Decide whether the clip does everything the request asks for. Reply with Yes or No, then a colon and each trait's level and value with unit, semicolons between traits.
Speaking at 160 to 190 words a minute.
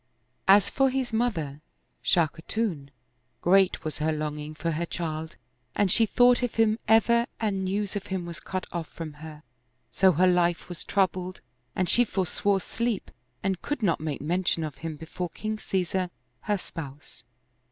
Yes: average, 165 wpm